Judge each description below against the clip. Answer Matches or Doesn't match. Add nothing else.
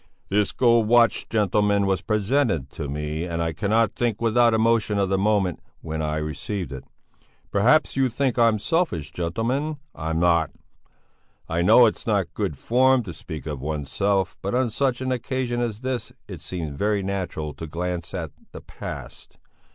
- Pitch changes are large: Matches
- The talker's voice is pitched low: Matches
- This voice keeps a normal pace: Matches